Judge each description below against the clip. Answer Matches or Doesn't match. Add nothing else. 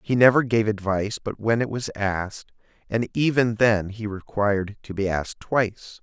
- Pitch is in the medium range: Doesn't match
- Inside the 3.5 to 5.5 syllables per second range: Matches